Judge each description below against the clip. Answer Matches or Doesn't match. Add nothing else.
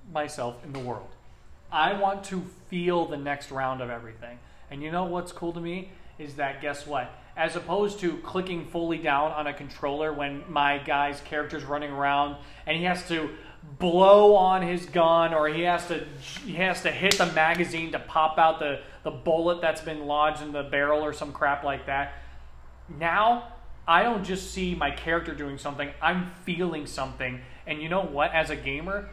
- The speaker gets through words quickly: Doesn't match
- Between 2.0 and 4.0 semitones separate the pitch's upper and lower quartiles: Matches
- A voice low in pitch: Doesn't match